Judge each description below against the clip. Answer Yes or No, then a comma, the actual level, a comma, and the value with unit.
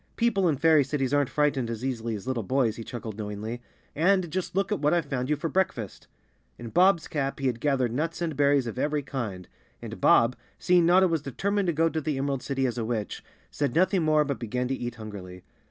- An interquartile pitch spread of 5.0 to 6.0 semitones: Yes, wide, 5.4 semitones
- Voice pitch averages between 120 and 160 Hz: Yes, medium, 140 Hz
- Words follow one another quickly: Yes, fast, 220 wpm